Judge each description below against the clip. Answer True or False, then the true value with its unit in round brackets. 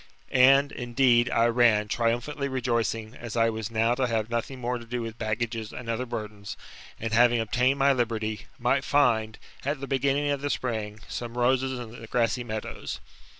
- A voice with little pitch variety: True (2.3 semitones)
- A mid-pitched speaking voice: False (120 Hz)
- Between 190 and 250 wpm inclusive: False (180 wpm)